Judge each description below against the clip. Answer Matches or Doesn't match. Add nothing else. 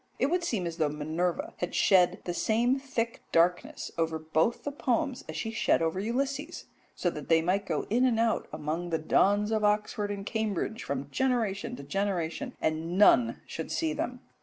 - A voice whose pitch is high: Matches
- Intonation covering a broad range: Matches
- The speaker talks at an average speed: Matches